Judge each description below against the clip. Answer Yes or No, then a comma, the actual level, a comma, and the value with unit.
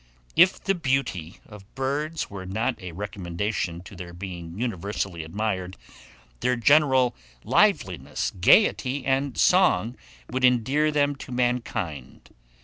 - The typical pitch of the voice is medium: No, low, 115 Hz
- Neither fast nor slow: No, slow, 120 wpm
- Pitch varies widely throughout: Yes, wide, 6.5 semitones